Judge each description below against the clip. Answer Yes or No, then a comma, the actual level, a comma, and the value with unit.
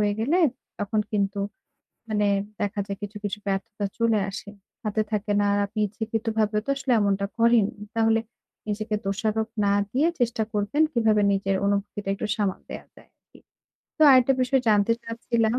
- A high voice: Yes, high, 215 Hz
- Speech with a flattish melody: Yes, narrow, 2.1 semitones